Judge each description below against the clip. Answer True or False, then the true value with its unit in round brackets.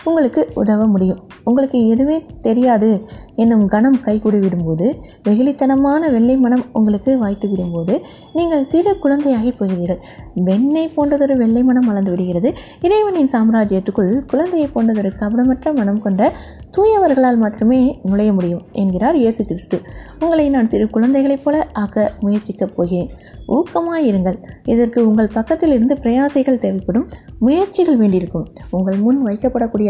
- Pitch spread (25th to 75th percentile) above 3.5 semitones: True (5.0 semitones)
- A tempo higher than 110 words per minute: True (120 wpm)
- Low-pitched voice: False (235 Hz)